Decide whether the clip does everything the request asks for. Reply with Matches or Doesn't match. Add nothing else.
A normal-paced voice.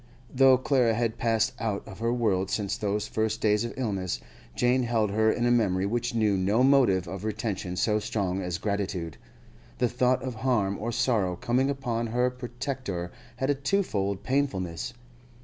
Matches